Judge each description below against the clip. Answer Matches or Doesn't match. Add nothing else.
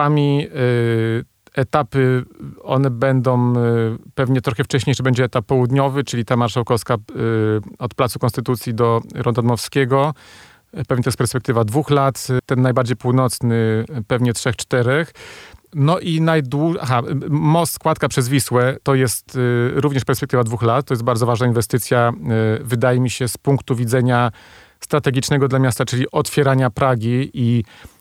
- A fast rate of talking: Doesn't match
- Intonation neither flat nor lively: Doesn't match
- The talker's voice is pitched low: Matches